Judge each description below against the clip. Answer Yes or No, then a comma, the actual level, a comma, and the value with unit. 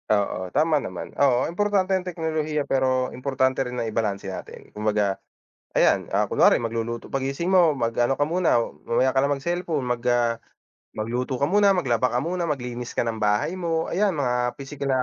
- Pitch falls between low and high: No, low, 130 Hz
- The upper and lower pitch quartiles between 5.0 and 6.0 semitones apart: Yes, wide, 5.4 semitones